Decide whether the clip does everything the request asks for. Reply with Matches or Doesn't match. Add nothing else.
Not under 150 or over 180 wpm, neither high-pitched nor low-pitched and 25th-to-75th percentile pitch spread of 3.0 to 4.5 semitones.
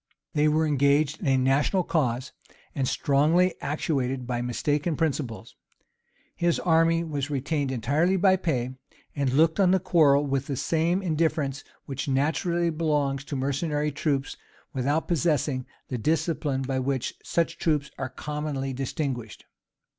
Doesn't match